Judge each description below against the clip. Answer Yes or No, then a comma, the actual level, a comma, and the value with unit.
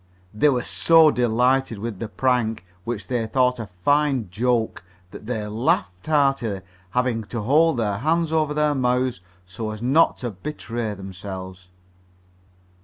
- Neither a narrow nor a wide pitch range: Yes, average, 4.3 semitones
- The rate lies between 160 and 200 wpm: No, average, 145 wpm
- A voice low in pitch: Yes, low, 120 Hz